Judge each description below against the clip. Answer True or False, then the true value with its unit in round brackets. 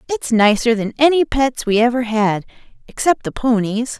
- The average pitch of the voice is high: True (235 Hz)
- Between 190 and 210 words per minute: False (165 wpm)